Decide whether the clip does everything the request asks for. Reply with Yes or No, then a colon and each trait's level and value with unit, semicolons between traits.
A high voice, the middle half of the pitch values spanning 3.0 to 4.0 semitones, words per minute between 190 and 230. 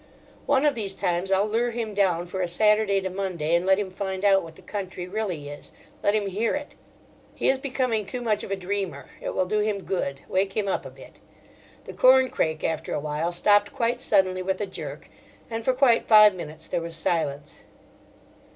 Yes: high, 195 Hz; average, 3.5 semitones; average, 200 wpm